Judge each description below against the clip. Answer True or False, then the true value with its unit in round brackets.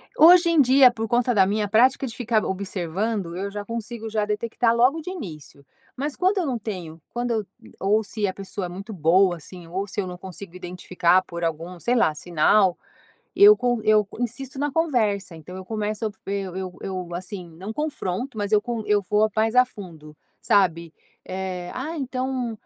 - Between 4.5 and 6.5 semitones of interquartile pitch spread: True (4.8 semitones)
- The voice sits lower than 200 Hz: False (210 Hz)